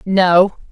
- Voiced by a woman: Yes, female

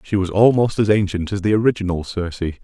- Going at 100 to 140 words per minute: No, fast, 205 wpm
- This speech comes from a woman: No, male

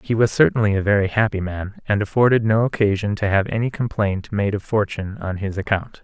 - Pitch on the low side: Yes, low, 105 Hz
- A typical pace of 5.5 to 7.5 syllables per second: Yes, 5.7 syllables/s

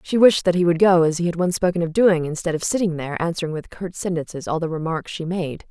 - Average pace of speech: No, fast, 275 wpm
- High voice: No, medium, 170 Hz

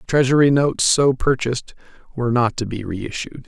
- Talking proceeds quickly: No, average, 155 wpm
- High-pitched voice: No, low, 125 Hz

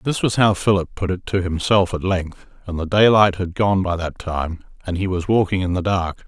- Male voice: Yes, male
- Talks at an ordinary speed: No, fast, 240 wpm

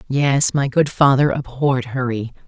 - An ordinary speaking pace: Yes, average, 145 wpm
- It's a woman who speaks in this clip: Yes, female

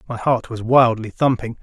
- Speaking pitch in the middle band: No, low, 120 Hz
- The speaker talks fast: No, average, 185 wpm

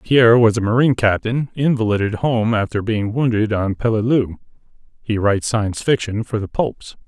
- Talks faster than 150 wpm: Yes, average, 160 wpm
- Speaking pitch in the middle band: No, low, 110 Hz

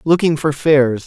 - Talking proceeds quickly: No, average, 170 wpm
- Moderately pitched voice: Yes, medium, 145 Hz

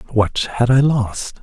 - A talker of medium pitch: No, low, 120 Hz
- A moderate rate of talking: Yes, average, 170 wpm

